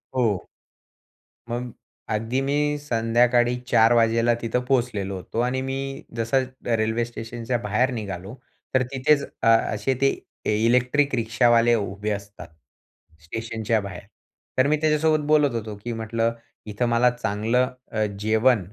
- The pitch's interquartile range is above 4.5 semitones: No, narrow, 2.6 semitones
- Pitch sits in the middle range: No, low, 115 Hz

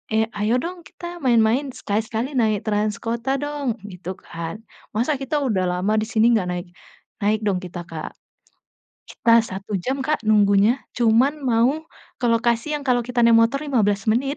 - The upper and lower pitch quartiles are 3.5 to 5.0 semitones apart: Yes, average, 4.2 semitones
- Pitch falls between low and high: No, high, 230 Hz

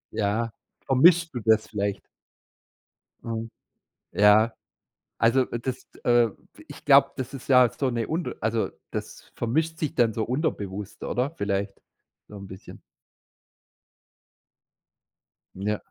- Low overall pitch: Yes, low, 115 Hz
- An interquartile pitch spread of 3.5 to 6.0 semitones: Yes, average, 3.8 semitones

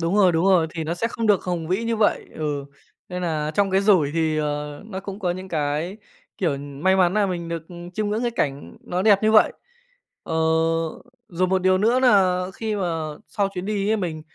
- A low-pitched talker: No, medium, 185 Hz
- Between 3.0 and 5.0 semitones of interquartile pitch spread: Yes, average, 3.9 semitones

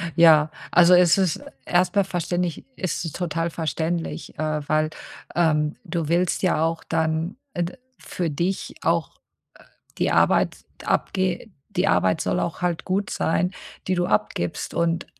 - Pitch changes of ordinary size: No, narrow, 2.2 semitones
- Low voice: No, medium, 170 Hz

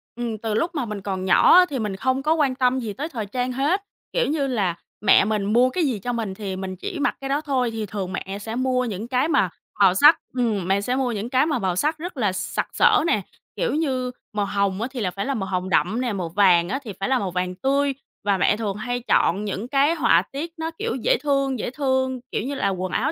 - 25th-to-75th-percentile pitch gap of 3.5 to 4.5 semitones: No, wide, 5.6 semitones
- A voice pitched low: No, high, 240 Hz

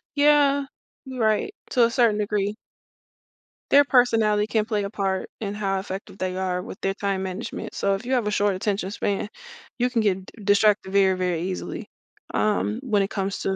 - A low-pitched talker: No, high, 205 Hz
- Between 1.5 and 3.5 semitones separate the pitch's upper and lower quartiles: Yes, average, 2.7 semitones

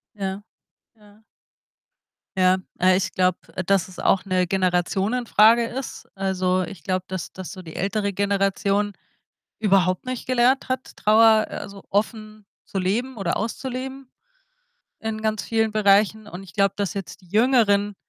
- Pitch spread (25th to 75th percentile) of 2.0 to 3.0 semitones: Yes, average, 2.7 semitones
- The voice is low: No, high, 200 Hz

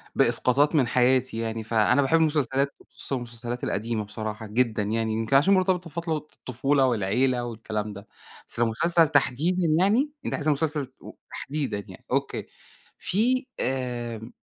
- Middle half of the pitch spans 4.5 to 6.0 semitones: Yes, average, 5.2 semitones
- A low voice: Yes, low, 130 Hz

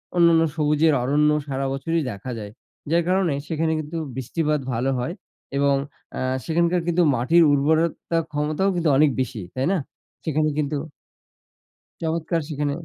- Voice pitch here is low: No, medium, 155 Hz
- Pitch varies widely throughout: No, average, 3.0 semitones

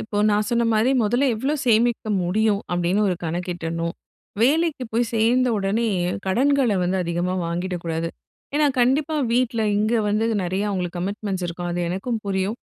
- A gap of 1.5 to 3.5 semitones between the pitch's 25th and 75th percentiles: No, average, 5.1 semitones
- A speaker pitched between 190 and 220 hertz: Yes, high, 210 Hz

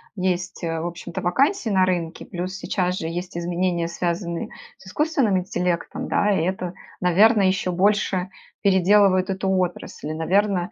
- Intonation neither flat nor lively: No, narrow, 1.9 semitones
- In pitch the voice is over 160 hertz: Yes, medium, 185 Hz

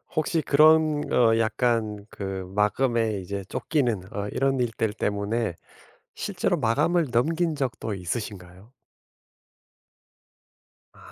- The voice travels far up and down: Yes, wide, 5.7 semitones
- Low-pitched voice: Yes, low, 115 Hz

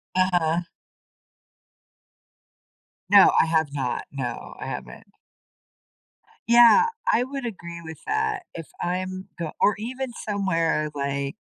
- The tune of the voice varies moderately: No, wide, 6.8 semitones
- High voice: No, medium, 180 Hz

